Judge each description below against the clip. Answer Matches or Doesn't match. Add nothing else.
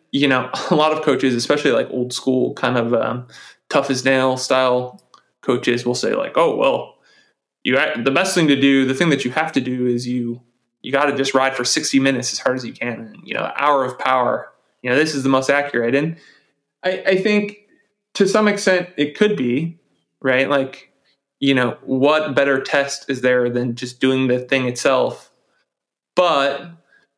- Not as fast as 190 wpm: Doesn't match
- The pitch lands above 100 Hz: Matches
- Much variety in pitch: Doesn't match